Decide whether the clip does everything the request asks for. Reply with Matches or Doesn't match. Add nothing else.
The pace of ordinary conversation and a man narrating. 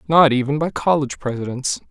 Matches